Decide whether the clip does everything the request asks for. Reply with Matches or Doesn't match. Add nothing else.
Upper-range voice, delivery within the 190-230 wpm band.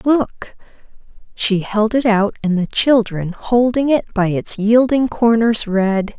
Doesn't match